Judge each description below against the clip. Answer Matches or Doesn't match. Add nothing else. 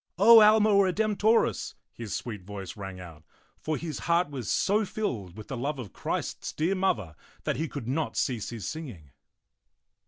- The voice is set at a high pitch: Doesn't match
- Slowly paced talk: Doesn't match